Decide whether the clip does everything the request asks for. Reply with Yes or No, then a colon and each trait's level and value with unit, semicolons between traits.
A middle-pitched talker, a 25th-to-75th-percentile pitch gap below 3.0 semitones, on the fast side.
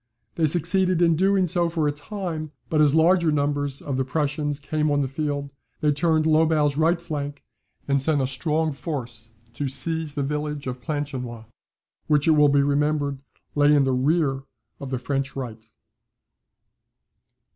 No: medium, 145 Hz; narrow, 2.4 semitones; average, 165 wpm